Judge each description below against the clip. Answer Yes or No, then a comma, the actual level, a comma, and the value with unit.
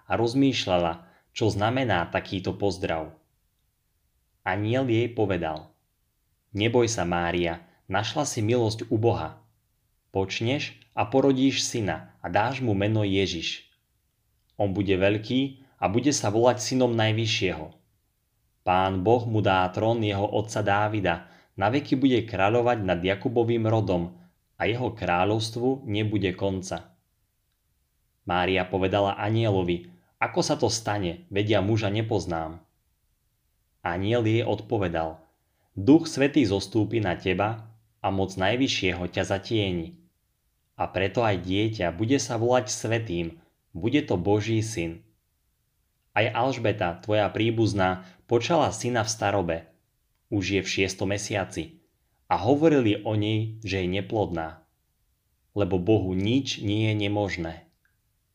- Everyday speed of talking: Yes, average, 120 wpm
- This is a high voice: No, low, 105 Hz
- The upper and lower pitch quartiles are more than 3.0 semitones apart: Yes, average, 3.7 semitones